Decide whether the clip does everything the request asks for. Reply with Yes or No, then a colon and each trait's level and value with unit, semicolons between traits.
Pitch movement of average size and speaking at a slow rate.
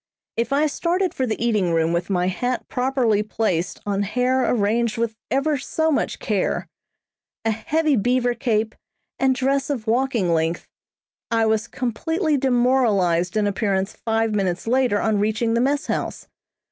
No: average, 4.2 semitones; average, 155 wpm